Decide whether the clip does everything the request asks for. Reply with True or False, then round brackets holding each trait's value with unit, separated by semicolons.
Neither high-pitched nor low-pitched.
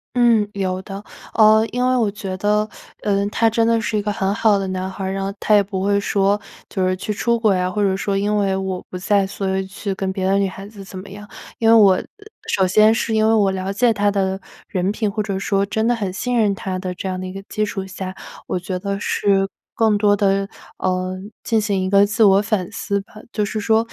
False (200 Hz)